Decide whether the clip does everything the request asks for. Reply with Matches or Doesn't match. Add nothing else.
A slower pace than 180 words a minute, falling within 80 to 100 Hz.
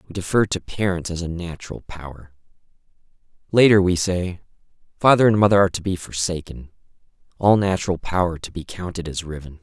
Matches